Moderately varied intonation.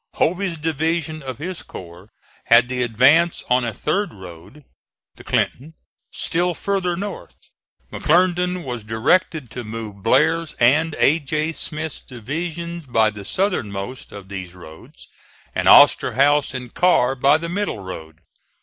No: wide, 7.0 semitones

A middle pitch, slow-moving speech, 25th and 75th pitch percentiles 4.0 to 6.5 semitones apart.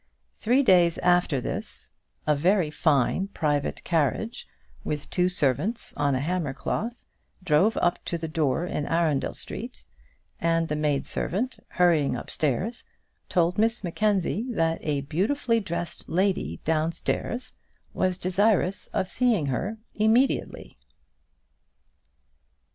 Yes: medium, 175 Hz; slow, 120 wpm; average, 5.1 semitones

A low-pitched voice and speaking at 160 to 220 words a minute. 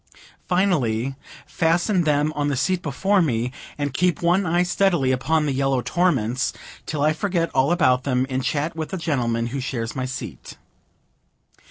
No: medium, 145 Hz; average, 165 wpm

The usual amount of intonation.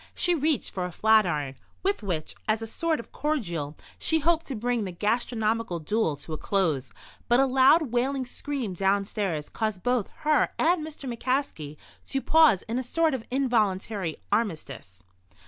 No: wide, 6.8 semitones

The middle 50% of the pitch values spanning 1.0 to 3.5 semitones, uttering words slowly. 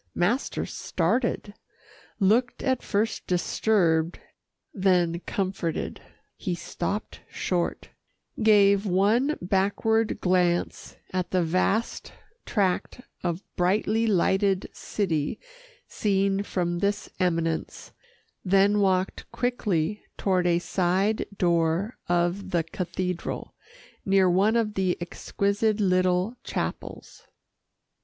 Yes: average, 2.8 semitones; slow, 95 wpm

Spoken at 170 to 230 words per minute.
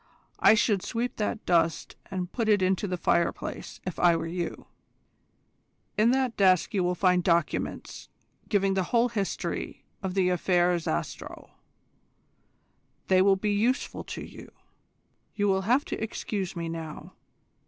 No: average, 150 wpm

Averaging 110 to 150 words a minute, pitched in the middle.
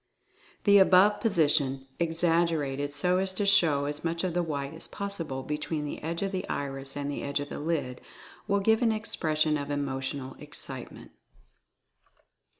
No: average, 160 wpm; medium, 155 Hz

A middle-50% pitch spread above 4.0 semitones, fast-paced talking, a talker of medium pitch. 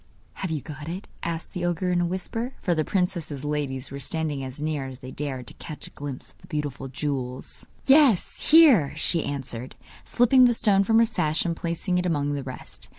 Yes: average, 4.7 semitones; fast, 210 wpm; medium, 160 Hz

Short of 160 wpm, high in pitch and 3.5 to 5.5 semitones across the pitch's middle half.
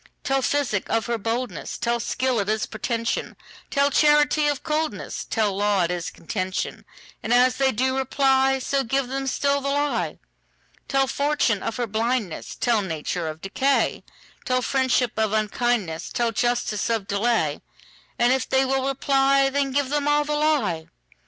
Yes: slow, 135 wpm; very high, 250 Hz; average, 4.1 semitones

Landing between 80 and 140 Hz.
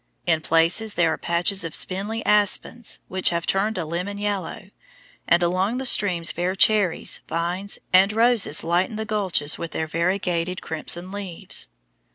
No: medium, 185 Hz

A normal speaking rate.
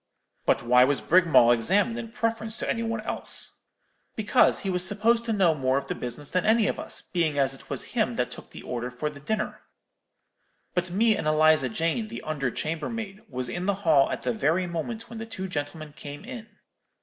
No: fast, 210 wpm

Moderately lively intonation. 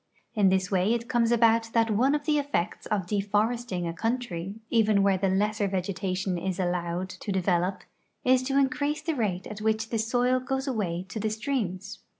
Yes: average, 4.2 semitones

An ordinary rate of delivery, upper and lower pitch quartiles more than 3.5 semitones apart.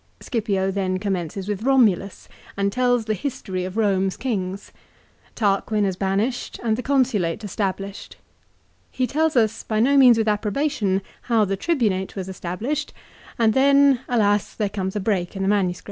Yes: average, 160 wpm; average, 4.1 semitones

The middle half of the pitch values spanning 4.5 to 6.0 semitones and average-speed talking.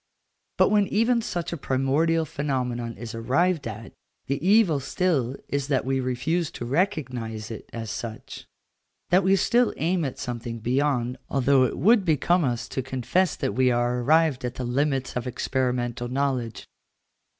Yes: average, 5.2 semitones; average, 160 wpm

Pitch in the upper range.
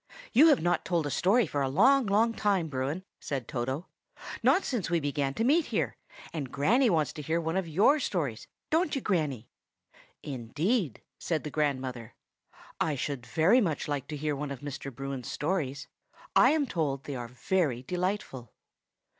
No: medium, 155 Hz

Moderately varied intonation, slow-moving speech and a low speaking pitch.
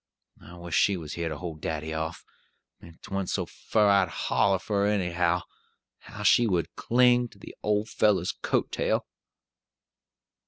No: average, 3.7 semitones; average, 160 wpm; very low, 95 Hz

